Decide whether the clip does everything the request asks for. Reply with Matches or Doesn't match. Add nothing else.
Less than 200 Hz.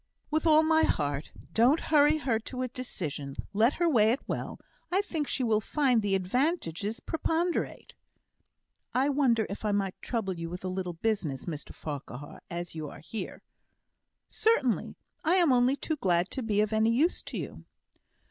Doesn't match